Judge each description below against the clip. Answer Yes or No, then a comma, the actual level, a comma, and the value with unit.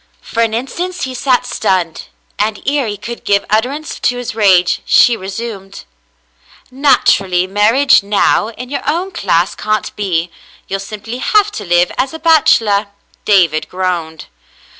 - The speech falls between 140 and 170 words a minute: Yes, average, 145 wpm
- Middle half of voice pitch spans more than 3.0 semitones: Yes, average, 5.1 semitones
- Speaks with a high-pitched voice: Yes, high, 215 Hz